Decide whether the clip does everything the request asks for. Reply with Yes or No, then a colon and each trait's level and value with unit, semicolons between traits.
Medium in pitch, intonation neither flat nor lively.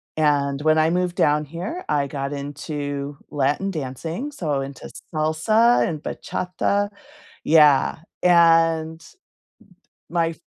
Yes: medium, 155 Hz; average, 3.0 semitones